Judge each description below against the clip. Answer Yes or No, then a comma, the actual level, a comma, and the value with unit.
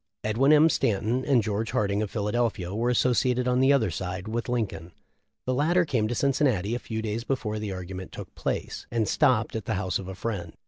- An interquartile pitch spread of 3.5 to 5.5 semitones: Yes, average, 3.9 semitones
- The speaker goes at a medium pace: No, fast, 210 wpm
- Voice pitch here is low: Yes, low, 110 Hz